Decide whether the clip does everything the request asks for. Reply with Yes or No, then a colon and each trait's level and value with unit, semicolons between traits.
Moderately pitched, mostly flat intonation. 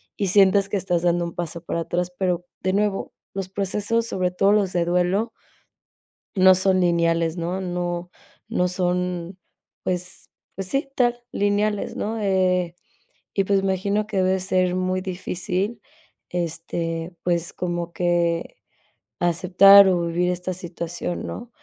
Yes: medium, 180 Hz; narrow, 2.0 semitones